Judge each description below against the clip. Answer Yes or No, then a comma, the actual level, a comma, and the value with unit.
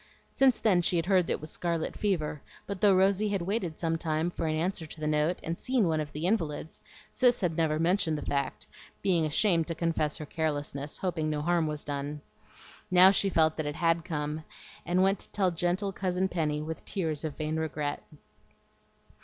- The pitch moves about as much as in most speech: Yes, average, 3.2 semitones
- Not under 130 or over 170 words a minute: No, fast, 205 wpm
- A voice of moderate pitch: Yes, medium, 165 Hz